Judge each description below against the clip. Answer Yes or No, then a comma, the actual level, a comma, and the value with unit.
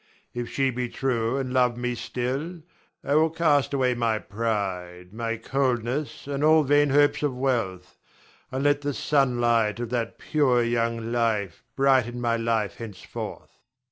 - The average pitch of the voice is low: Yes, low, 120 Hz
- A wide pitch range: No, average, 3.2 semitones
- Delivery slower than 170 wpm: Yes, average, 150 wpm